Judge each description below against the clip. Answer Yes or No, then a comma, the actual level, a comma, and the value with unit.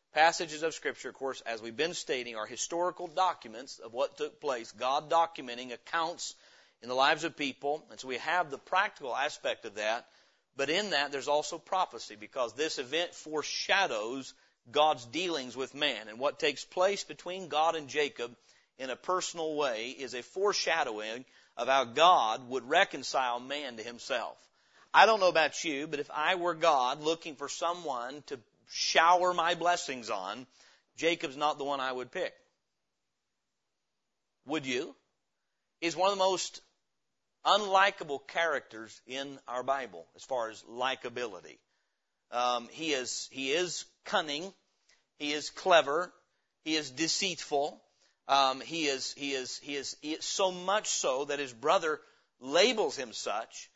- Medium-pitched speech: Yes, medium, 150 Hz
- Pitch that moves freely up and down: No, average, 4.7 semitones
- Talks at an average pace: Yes, average, 155 wpm